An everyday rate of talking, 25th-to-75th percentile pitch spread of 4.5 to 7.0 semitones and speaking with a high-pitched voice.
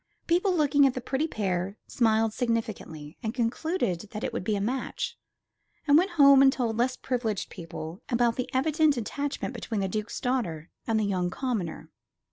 Yes: average, 175 wpm; average, 5.0 semitones; high, 235 Hz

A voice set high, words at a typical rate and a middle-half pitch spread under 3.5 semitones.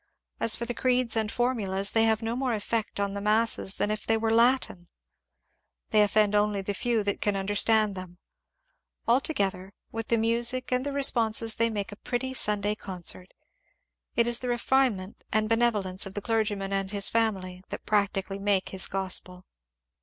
Yes: high, 215 Hz; average, 185 wpm; average, 2.8 semitones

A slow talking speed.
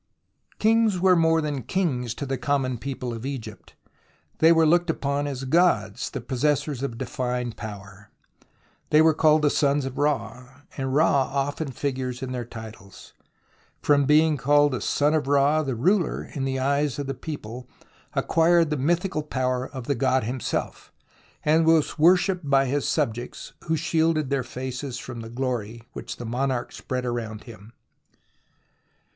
No: average, 165 wpm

